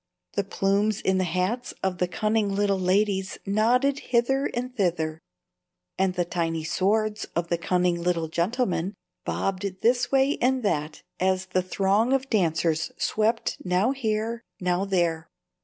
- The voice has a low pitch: No, high, 195 Hz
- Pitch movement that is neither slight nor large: Yes, average, 4.0 semitones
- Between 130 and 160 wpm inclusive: Yes, average, 145 wpm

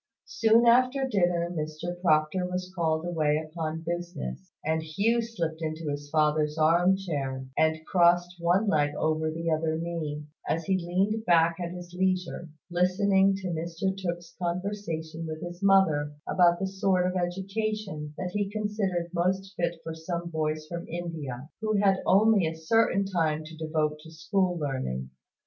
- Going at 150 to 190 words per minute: Yes, average, 160 wpm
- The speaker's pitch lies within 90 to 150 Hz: No, medium, 170 Hz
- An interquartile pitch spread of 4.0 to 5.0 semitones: No, average, 3.3 semitones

